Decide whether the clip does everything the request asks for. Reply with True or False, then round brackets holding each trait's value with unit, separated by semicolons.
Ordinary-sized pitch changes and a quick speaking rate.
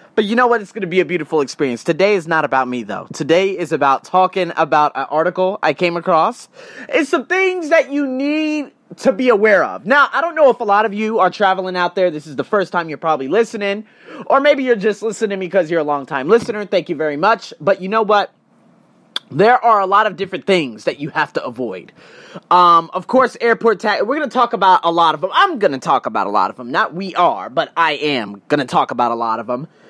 False (6.0 semitones; 255 wpm)